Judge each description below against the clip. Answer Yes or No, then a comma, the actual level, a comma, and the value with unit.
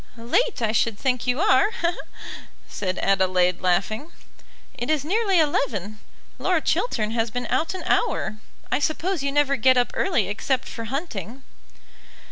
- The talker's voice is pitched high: Yes, very high, 250 Hz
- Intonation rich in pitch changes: Yes, wide, 6.4 semitones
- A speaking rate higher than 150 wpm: No, average, 145 wpm